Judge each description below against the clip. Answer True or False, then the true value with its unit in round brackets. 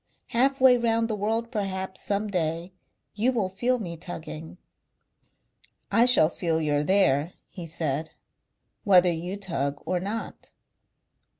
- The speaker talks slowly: True (130 wpm)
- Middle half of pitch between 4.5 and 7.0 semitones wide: True (5.4 semitones)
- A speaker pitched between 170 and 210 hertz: True (190 Hz)